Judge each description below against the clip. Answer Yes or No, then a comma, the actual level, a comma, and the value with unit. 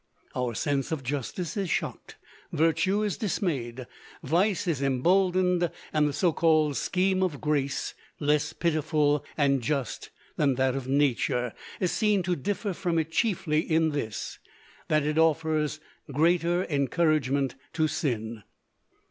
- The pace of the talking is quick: No, slow, 135 wpm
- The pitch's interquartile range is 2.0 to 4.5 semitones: Yes, average, 4.0 semitones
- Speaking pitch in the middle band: Yes, medium, 155 Hz